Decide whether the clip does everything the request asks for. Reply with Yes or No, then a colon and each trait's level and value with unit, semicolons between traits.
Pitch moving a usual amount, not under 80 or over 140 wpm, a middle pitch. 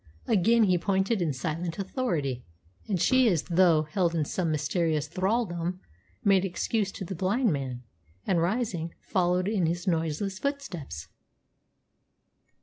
Yes: average, 3.4 semitones; slow, 135 wpm; medium, 180 Hz